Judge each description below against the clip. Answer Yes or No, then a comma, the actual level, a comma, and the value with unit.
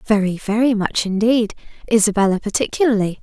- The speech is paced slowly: Yes, slow, 110 wpm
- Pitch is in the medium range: No, high, 215 Hz